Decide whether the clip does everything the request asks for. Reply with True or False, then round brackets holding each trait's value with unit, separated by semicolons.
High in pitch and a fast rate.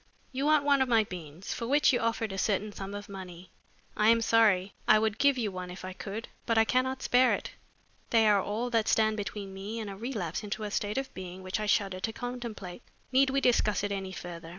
True (215 Hz; 235 wpm)